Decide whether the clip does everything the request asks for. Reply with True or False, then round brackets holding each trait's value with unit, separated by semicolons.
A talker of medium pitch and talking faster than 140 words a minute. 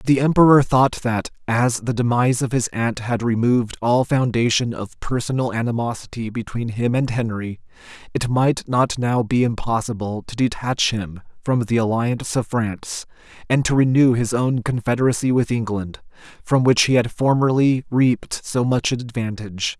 False (120 Hz; 160 wpm)